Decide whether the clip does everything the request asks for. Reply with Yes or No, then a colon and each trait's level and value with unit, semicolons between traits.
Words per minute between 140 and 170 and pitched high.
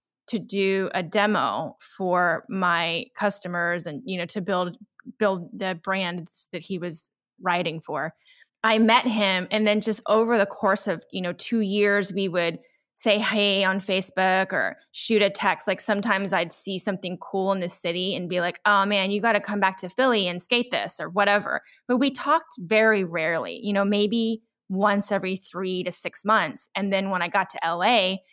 No: average, 195 wpm; high, 195 Hz